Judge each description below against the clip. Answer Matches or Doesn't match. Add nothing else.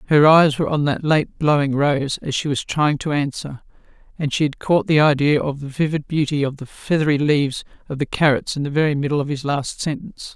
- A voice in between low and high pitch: Matches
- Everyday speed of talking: Doesn't match